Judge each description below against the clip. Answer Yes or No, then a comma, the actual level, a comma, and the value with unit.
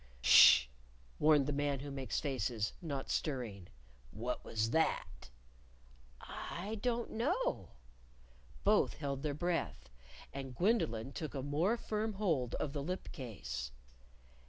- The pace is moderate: No, slow, 130 wpm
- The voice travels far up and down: Yes, wide, 6.1 semitones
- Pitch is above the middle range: No, medium, 140 Hz